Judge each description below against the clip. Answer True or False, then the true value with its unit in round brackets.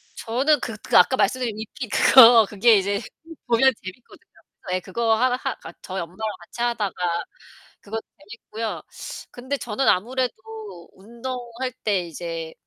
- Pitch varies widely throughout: False (3.9 semitones)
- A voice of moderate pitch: False (225 Hz)